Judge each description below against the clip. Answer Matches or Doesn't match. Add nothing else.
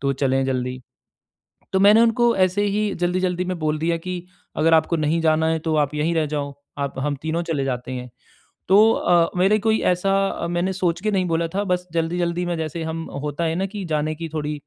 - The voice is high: Doesn't match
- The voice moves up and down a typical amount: Matches